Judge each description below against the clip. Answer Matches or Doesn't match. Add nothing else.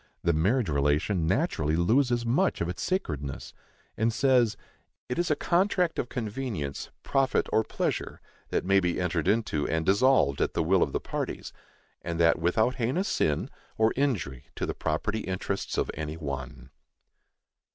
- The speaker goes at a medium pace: Matches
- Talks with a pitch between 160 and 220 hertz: Doesn't match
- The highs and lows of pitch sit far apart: Matches